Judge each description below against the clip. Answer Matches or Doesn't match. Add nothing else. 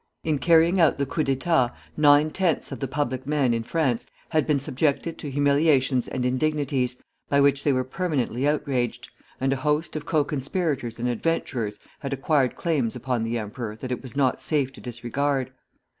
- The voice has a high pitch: Doesn't match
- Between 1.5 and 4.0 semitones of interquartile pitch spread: Matches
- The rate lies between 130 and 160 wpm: Doesn't match